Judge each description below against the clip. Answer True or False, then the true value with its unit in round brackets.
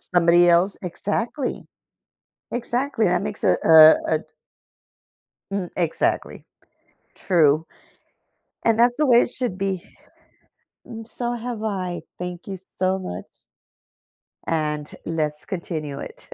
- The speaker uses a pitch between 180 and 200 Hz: True (185 Hz)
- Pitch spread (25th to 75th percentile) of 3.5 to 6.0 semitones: True (5.5 semitones)